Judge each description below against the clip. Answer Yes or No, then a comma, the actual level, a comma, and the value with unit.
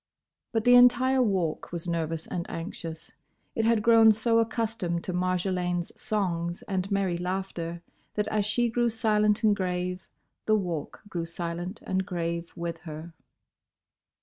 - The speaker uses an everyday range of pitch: Yes, average, 4.2 semitones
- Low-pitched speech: No, medium, 185 Hz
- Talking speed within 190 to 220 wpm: No, average, 145 wpm